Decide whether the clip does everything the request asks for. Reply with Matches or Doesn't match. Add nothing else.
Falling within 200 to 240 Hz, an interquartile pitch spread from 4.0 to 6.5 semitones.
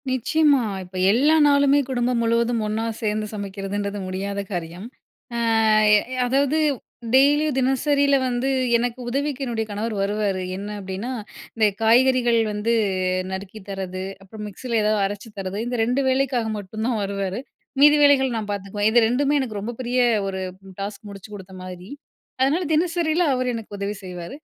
Matches